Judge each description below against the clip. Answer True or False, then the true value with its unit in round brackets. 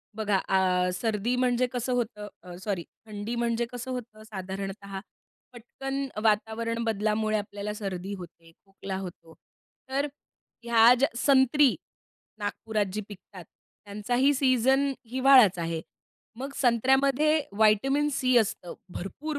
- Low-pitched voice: False (220 Hz)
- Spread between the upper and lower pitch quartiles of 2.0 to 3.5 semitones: False (4.2 semitones)